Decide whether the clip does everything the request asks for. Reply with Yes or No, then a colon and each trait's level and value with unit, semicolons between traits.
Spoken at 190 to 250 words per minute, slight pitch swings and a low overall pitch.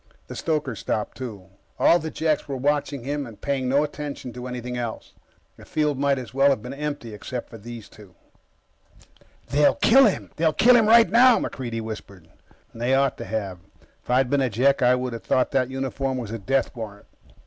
No: average, 200 wpm; average, 3.7 semitones; low, 130 Hz